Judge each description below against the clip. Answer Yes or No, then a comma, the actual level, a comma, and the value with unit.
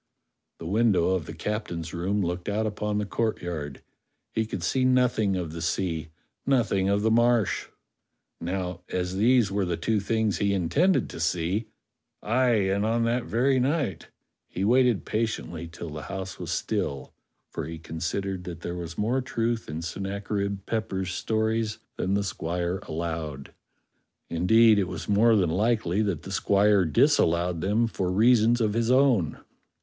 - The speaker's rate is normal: Yes, average, 165 wpm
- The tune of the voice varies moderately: Yes, average, 4.4 semitones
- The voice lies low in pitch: Yes, low, 100 Hz